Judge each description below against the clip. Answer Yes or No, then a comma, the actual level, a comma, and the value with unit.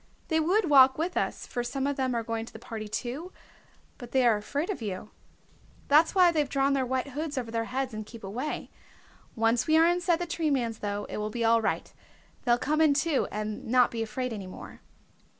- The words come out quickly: Yes, fast, 220 wpm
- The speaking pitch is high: Yes, very high, 255 Hz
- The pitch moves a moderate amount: Yes, average, 5.0 semitones